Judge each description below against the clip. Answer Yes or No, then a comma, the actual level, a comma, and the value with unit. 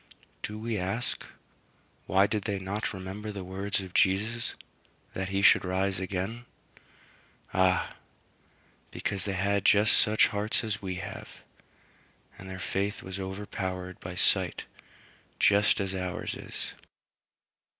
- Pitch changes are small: Yes, narrow, 1.7 semitones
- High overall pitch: No, very low, 95 Hz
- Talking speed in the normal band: No, slow, 130 wpm